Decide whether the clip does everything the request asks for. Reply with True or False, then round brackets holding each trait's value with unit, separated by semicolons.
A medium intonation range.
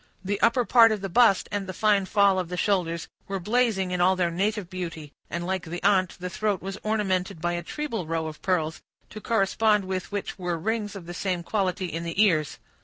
True (3.1 semitones)